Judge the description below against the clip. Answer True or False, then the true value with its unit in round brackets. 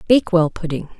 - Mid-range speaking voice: True (175 Hz)